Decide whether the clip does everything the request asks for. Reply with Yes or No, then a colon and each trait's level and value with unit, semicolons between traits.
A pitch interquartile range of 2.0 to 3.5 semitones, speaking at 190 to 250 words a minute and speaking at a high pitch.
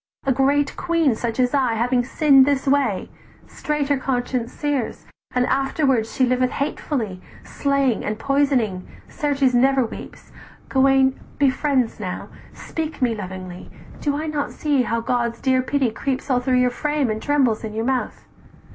No: average, 2.9 semitones; average, 160 wpm; very high, 260 Hz